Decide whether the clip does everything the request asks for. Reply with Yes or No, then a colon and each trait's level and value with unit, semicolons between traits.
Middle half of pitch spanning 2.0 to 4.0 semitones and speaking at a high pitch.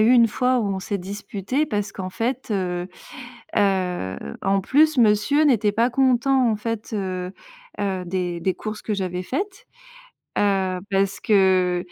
No: average, 4.4 semitones; high, 205 Hz